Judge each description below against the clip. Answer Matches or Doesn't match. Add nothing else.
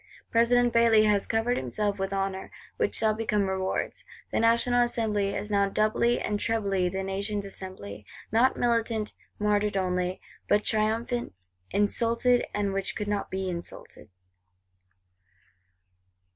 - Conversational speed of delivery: Doesn't match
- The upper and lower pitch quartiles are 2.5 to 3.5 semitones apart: Matches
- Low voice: Doesn't match